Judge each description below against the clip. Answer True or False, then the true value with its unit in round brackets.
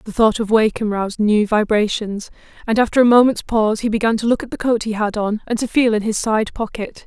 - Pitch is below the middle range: False (220 Hz)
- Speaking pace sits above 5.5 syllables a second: True (5.8 syllables/s)